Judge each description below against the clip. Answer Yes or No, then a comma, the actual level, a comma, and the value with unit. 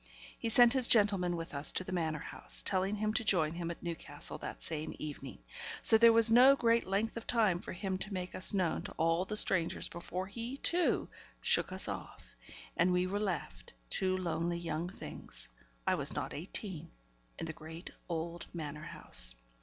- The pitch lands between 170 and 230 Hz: Yes, medium, 185 Hz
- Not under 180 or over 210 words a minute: Yes, average, 190 wpm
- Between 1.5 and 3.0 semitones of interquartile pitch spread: No, average, 4.2 semitones